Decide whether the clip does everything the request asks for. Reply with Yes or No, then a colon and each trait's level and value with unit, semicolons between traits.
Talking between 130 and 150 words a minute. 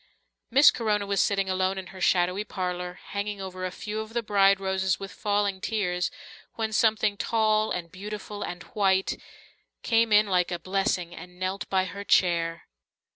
No: average, 170 wpm